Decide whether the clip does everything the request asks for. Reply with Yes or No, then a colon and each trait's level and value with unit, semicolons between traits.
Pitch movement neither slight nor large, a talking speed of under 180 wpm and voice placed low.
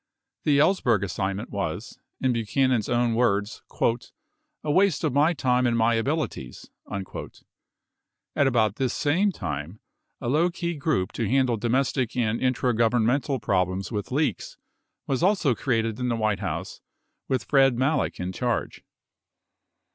Yes: average, 4.3 semitones; average, 145 wpm; low, 125 Hz